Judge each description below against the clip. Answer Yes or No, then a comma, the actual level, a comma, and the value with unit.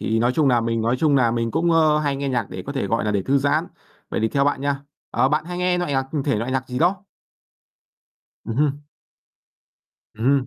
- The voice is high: No, low, 135 Hz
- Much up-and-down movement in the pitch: No, average, 4.3 semitones